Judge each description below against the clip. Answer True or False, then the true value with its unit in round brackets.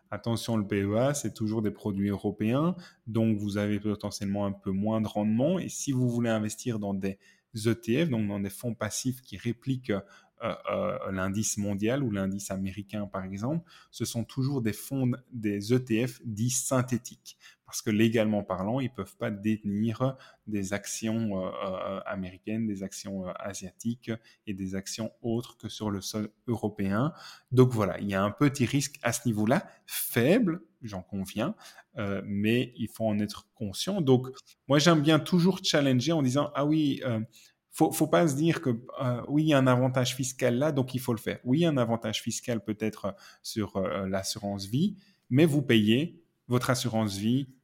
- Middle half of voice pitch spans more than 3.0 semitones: True (4.0 semitones)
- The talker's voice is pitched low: True (115 Hz)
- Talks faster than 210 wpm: False (185 wpm)